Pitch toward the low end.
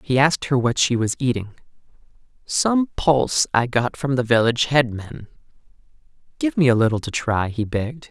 Yes: low, 125 Hz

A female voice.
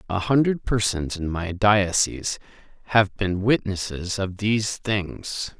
No: male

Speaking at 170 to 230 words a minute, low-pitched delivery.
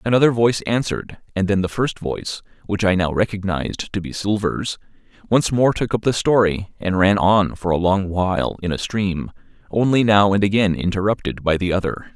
Yes: average, 190 wpm; low, 100 Hz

